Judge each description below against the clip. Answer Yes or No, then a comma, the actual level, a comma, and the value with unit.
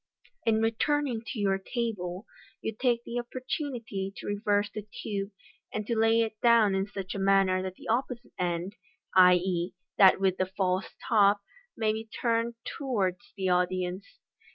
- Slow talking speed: No, average, 155 wpm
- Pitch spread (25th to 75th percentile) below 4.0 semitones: Yes, average, 3.4 semitones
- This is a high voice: Yes, high, 205 Hz